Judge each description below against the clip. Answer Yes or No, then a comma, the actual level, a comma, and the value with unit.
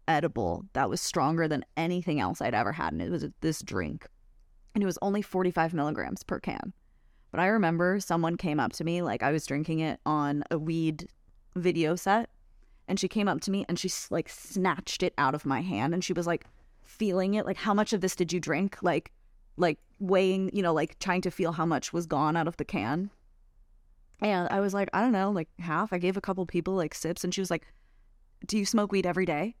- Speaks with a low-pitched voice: No, medium, 180 Hz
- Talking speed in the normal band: No, fast, 230 wpm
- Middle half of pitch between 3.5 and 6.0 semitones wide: No, average, 3.1 semitones